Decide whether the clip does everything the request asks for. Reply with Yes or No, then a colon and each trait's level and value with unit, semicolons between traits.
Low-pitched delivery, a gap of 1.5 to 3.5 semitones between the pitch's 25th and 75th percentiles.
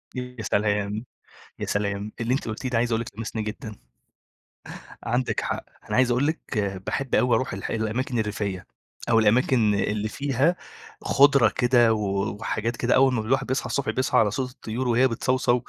Yes: low, 115 Hz; average, 3.1 semitones